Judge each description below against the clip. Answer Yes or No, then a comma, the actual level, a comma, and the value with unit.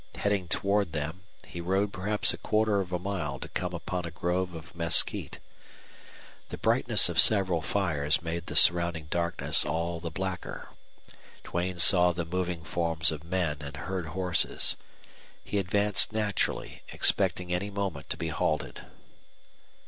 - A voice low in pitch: Yes, very low, 90 Hz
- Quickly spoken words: No, average, 150 wpm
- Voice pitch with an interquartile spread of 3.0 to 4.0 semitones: No, narrow, 2.6 semitones